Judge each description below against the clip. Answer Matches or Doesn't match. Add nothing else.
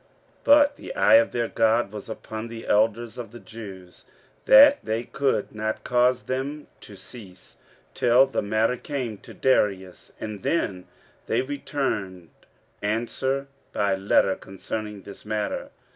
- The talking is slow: Doesn't match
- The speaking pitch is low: Matches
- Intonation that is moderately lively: Matches